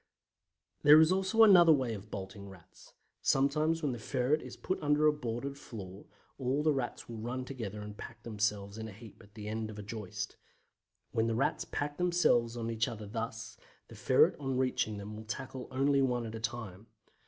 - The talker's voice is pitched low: Yes, low, 120 Hz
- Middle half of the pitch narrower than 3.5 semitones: No, average, 4.5 semitones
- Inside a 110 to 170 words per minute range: No, average, 200 wpm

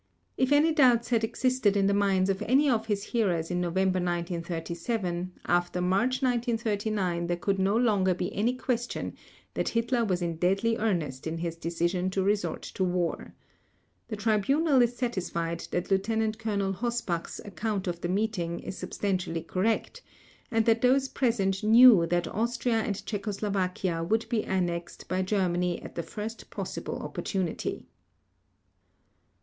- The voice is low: No, high, 200 Hz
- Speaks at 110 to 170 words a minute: Yes, average, 150 wpm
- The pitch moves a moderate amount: Yes, average, 4.3 semitones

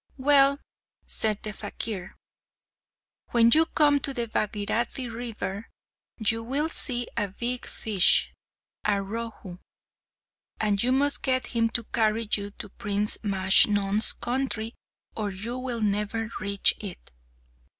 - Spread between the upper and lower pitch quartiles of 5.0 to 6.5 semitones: No, average, 3.1 semitones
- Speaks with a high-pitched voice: Yes, high, 225 Hz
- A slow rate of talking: Yes, slow, 125 wpm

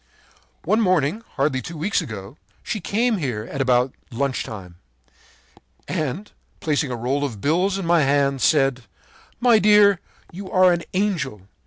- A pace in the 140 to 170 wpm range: Yes, average, 150 wpm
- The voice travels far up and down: Yes, wide, 6.7 semitones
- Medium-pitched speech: Yes, medium, 150 Hz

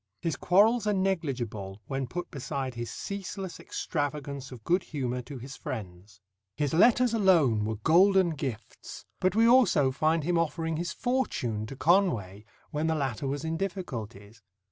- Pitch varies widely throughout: Yes, wide, 7.2 semitones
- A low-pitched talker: No, medium, 150 Hz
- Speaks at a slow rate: No, average, 155 wpm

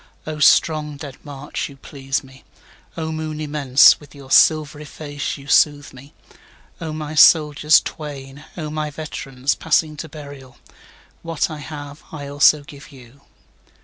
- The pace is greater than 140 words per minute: No, slow, 135 wpm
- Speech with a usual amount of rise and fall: No, narrow, 1.7 semitones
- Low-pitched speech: No, medium, 145 Hz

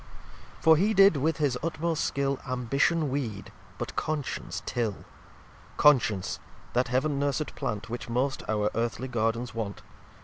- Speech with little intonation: No, average, 4.4 semitones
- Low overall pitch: Yes, low, 130 Hz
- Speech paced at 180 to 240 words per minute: No, average, 140 wpm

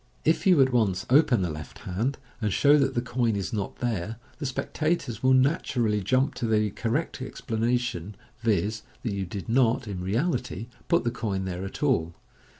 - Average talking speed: Yes, average, 180 wpm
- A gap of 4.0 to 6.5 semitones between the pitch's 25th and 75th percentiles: Yes, average, 4.6 semitones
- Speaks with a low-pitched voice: Yes, low, 115 Hz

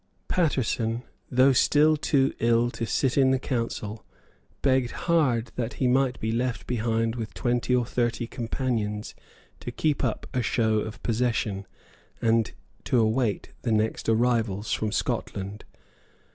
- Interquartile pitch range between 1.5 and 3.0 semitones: Yes, narrow, 2.5 semitones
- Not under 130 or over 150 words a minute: Yes, average, 140 wpm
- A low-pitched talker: Yes, low, 120 Hz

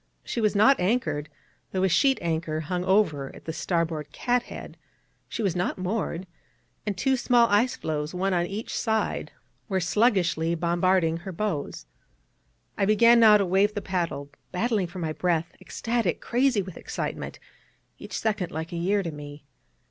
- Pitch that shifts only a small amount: No, average, 4.4 semitones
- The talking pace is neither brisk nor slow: Yes, average, 165 wpm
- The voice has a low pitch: No, medium, 185 Hz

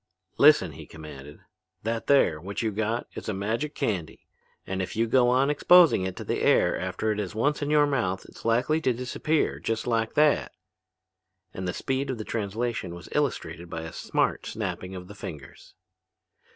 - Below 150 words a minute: No, average, 185 wpm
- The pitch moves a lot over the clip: Yes, wide, 6.0 semitones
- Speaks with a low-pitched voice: Yes, low, 110 Hz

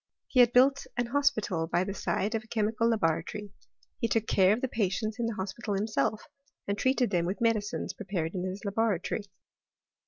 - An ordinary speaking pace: Yes, average, 185 wpm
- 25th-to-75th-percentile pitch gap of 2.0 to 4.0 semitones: Yes, average, 3.2 semitones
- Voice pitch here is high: Yes, high, 215 Hz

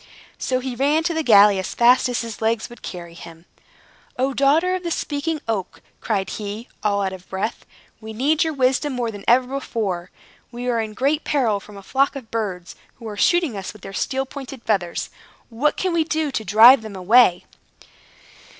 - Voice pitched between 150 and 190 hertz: No, high, 235 Hz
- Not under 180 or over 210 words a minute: Yes, average, 195 wpm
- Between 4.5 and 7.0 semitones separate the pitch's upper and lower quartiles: Yes, average, 5.2 semitones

